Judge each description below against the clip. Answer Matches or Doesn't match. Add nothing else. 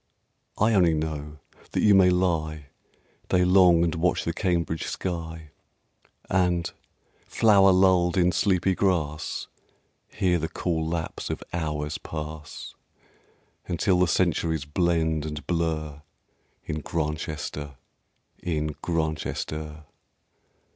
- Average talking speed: Doesn't match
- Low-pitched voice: Matches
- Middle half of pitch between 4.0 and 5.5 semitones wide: Doesn't match